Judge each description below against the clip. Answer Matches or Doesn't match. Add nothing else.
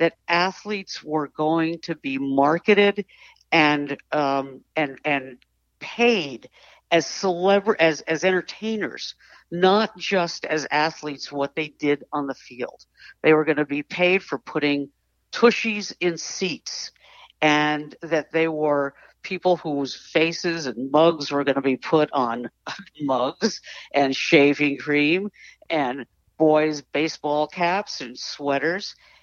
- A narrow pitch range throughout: Doesn't match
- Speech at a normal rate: Doesn't match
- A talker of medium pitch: Matches